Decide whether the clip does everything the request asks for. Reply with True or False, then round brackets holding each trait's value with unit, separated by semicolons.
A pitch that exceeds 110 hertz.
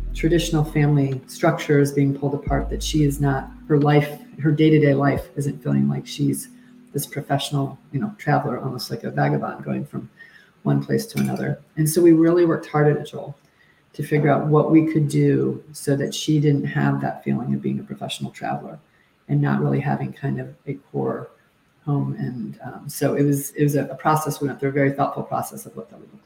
True (140 Hz)